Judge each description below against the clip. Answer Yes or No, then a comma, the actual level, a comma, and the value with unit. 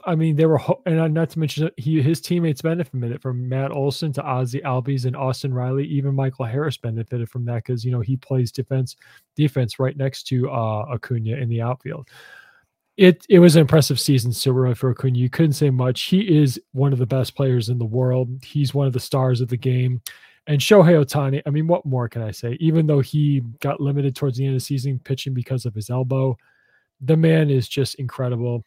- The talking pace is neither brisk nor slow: No, fast, 225 wpm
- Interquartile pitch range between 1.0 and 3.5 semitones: Yes, average, 2.8 semitones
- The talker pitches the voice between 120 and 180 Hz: Yes, low, 135 Hz